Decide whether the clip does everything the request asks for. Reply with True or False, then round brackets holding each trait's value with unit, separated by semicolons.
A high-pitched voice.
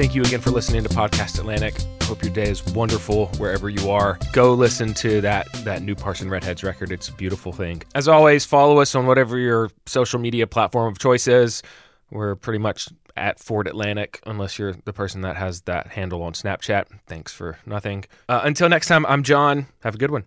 False (105 Hz)